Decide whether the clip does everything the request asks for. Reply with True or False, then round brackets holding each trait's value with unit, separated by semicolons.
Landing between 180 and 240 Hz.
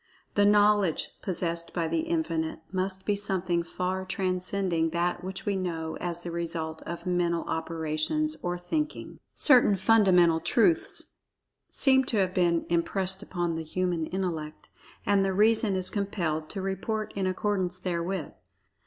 True (185 Hz)